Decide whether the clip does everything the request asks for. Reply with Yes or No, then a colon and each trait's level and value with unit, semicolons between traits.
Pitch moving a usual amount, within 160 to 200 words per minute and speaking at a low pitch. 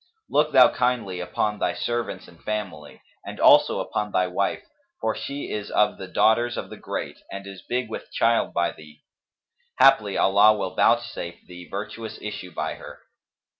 Yes: average, 4.1 semitones; average, 170 wpm; low, 105 Hz